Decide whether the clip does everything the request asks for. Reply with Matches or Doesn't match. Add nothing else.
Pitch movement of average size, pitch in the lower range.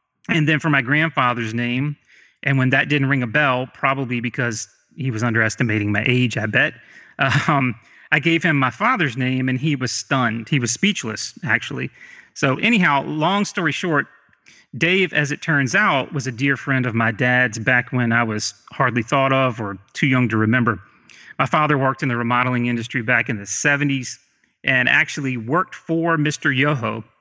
Matches